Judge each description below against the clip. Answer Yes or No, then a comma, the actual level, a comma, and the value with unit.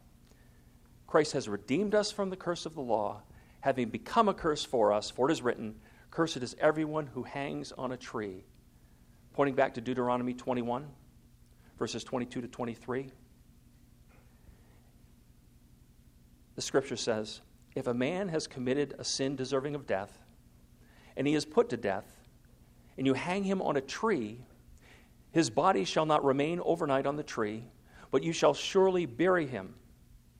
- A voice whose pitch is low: Yes, low, 130 Hz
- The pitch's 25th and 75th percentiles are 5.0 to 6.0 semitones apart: Yes, average, 5.3 semitones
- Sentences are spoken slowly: No, average, 155 wpm